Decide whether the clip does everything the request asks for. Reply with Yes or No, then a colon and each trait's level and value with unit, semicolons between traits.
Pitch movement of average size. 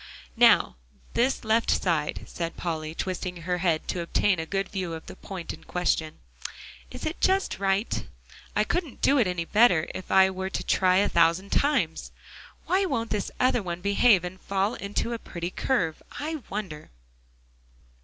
Yes: average, 4.3 semitones